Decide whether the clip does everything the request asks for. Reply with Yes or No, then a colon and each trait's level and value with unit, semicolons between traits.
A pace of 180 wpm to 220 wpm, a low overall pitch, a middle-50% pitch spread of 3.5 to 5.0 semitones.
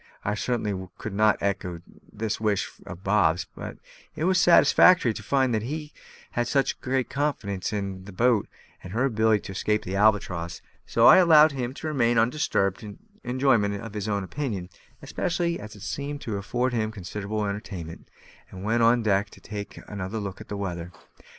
Yes: average, 185 wpm; low, 105 Hz; average, 4.2 semitones